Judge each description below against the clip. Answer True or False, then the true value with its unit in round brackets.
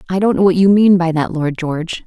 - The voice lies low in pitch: False (175 Hz)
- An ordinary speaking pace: False (290 wpm)